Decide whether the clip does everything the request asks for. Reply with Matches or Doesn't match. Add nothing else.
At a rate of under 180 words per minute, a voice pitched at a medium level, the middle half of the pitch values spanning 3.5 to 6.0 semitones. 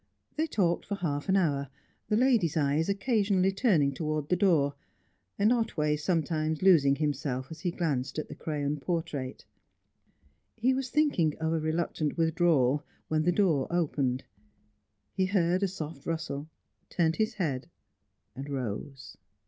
Matches